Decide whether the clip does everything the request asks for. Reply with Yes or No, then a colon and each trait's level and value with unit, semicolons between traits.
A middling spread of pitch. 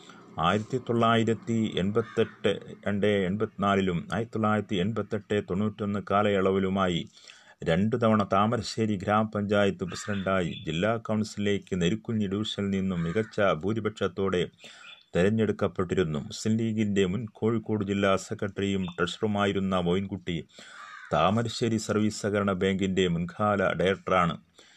No: narrow, 1.9 semitones